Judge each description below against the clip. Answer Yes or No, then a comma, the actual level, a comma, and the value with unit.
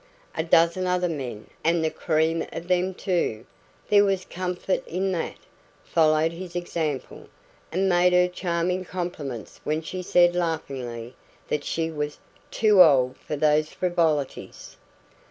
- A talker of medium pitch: Yes, medium, 170 Hz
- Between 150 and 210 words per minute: No, slow, 135 wpm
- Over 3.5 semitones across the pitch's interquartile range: No, average, 2.9 semitones